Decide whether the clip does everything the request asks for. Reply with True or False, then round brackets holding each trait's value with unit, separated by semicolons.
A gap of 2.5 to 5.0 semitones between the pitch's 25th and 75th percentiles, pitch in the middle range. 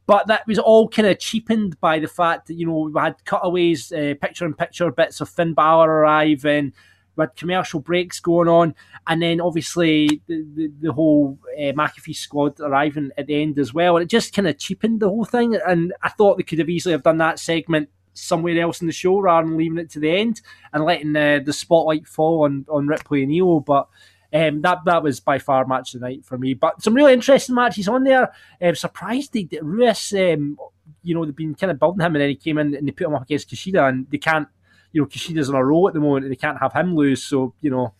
True (3.2 semitones; 160 Hz)